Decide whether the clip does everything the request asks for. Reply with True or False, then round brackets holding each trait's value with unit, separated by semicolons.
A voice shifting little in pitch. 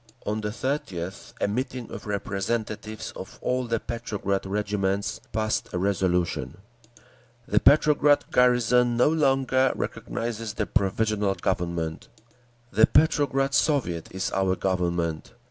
False (4.6 semitones)